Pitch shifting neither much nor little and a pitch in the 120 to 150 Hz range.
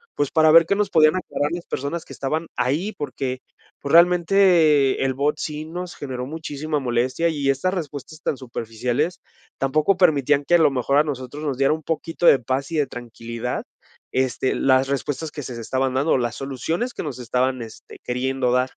Yes: average, 3.7 semitones; medium, 140 Hz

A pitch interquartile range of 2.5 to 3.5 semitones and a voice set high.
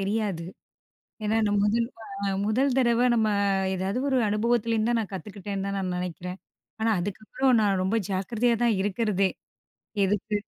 Yes: average, 2.9 semitones; high, 210 Hz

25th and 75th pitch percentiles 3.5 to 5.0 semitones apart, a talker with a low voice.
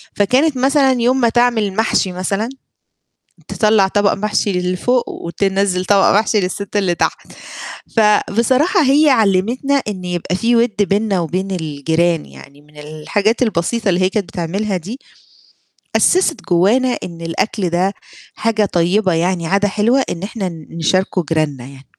No: average, 4.5 semitones; high, 195 Hz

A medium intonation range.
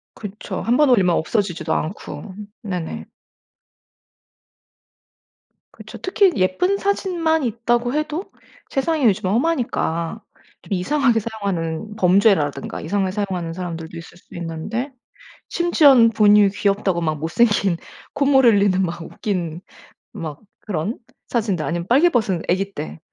No: wide, 5.9 semitones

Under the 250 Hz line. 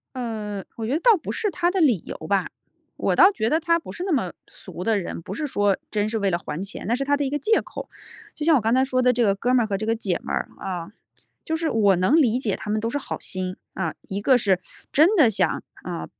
Yes: high, 230 Hz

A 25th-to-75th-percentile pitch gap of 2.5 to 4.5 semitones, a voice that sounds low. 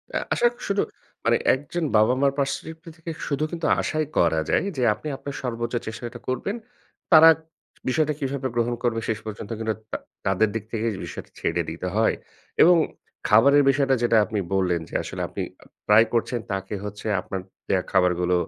No: average, 5.2 semitones; low, 120 Hz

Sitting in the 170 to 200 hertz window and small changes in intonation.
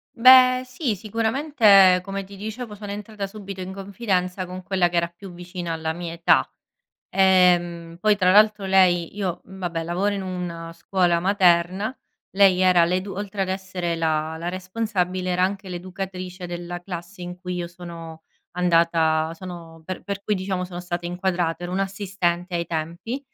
Yes: medium, 185 Hz; narrow, 2.3 semitones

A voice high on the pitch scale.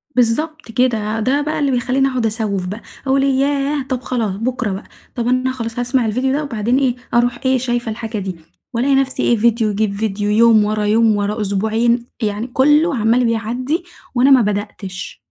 Yes: high, 235 Hz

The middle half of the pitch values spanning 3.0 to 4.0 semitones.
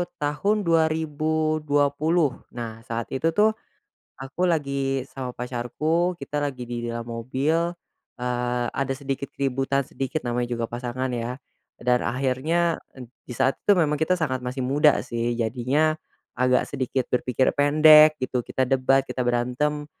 Yes: average, 3.7 semitones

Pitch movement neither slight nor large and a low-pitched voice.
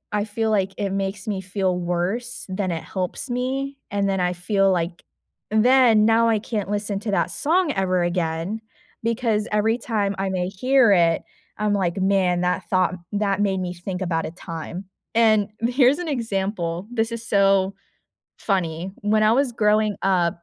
No: average, 3.3 semitones; high, 200 Hz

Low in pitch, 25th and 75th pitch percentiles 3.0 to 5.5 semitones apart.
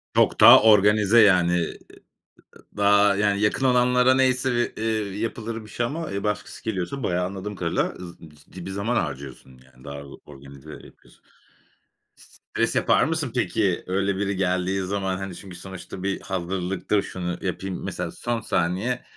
Yes: low, 100 Hz; average, 3.6 semitones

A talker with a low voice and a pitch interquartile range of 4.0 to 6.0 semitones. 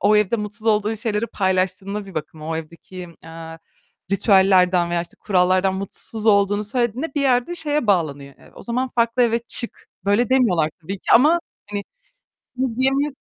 No: high, 205 Hz; average, 4.4 semitones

